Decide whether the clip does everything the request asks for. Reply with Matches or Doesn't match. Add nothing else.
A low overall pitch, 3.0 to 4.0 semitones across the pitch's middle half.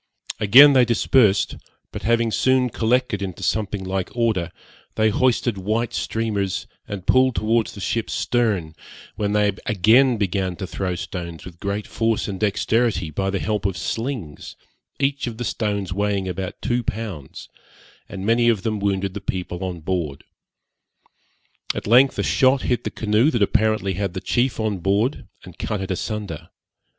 Matches